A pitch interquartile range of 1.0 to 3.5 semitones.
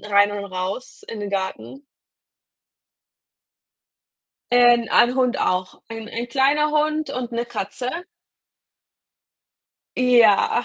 No: average, 3.9 semitones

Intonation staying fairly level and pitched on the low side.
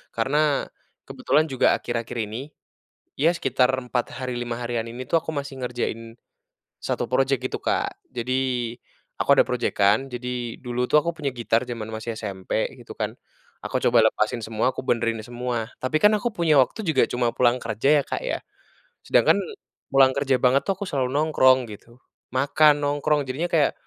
No: average, 3.5 semitones; low, 125 Hz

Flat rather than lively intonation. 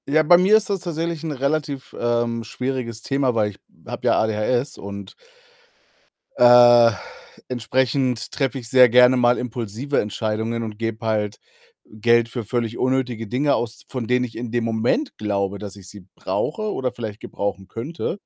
No: average, 3.1 semitones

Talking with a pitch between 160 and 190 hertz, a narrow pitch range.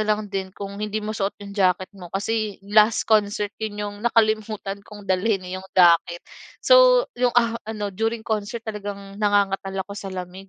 No: high, 205 Hz; narrow, 1.9 semitones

